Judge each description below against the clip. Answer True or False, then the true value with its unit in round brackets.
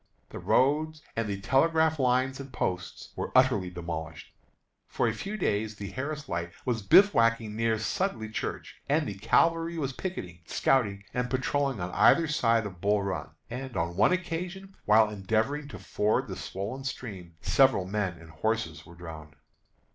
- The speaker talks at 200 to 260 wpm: False (160 wpm)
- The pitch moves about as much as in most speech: False (6.4 semitones)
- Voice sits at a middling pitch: False (115 Hz)